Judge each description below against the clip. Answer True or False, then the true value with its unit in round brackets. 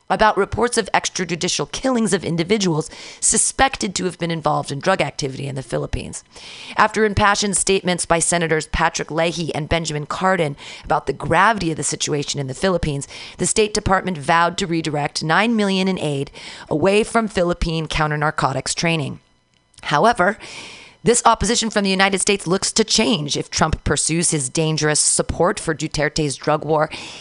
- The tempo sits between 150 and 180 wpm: True (160 wpm)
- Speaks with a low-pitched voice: False (170 Hz)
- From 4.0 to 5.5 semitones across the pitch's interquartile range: True (4.5 semitones)